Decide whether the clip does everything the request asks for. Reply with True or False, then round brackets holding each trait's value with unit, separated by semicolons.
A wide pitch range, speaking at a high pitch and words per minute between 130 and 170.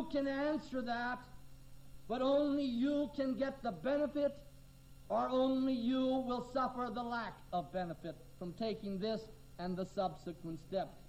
True (7.6 semitones; 235 Hz; 140 wpm)